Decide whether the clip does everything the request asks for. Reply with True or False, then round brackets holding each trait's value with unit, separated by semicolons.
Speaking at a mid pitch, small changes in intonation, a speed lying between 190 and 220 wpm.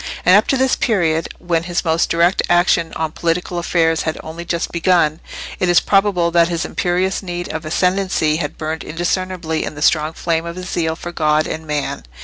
True (170 Hz; 1.9 semitones; 195 wpm)